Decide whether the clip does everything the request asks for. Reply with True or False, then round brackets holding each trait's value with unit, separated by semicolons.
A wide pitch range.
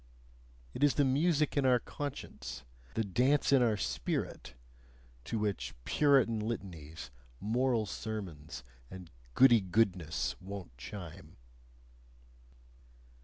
True (6.1 semitones)